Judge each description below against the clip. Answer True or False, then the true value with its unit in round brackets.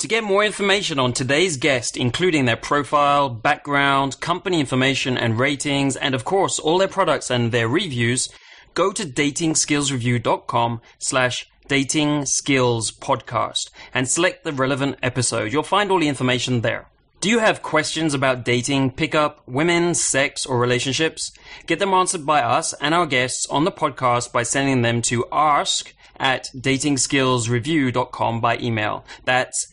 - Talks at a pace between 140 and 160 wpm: True (150 wpm)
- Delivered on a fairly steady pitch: False (3.9 semitones)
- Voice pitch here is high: False (135 Hz)